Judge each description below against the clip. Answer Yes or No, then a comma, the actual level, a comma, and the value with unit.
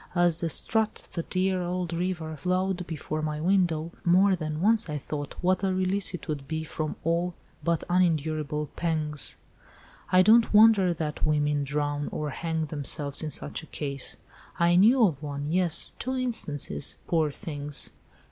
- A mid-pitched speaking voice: Yes, medium, 165 Hz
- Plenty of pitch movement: No, average, 3.5 semitones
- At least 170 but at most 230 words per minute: No, average, 150 wpm